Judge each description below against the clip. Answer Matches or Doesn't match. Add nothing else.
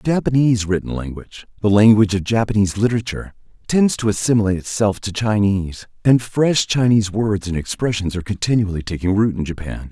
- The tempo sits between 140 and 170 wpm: Matches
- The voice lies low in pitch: Matches